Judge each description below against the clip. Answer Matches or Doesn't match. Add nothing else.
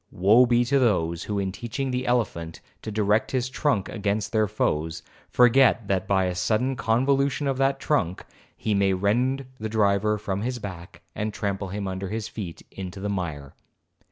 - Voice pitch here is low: Matches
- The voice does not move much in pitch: Doesn't match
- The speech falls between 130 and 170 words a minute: Doesn't match